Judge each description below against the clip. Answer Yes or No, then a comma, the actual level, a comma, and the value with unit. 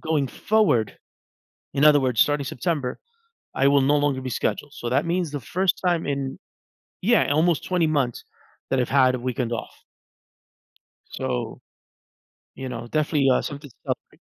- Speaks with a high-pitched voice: No, medium, 140 Hz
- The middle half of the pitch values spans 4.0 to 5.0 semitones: No, average, 3.4 semitones